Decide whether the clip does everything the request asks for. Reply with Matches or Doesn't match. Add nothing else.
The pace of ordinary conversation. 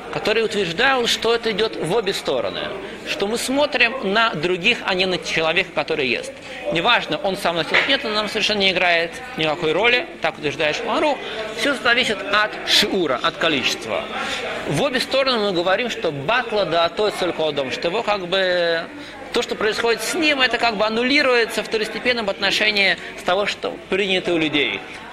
Doesn't match